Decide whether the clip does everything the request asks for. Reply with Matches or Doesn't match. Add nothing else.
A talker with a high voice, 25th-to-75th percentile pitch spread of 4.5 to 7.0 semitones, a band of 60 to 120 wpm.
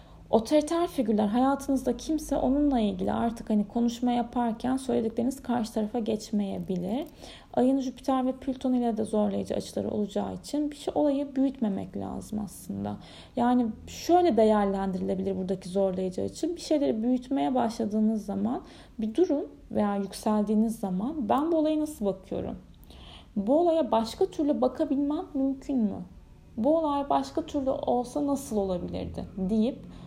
Doesn't match